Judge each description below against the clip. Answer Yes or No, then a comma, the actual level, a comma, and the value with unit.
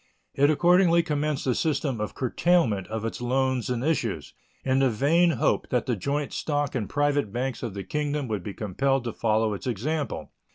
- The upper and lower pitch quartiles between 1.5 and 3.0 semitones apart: No, average, 4.8 semitones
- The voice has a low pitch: Yes, low, 130 Hz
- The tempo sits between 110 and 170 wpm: No, average, 190 wpm